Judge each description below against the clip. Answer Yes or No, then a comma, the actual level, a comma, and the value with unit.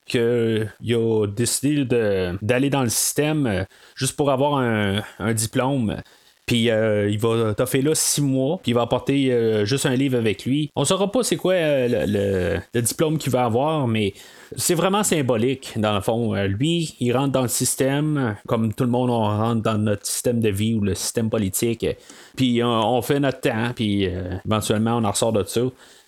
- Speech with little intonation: No, average, 3.8 semitones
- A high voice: No, low, 120 Hz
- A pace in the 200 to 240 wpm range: Yes, average, 210 wpm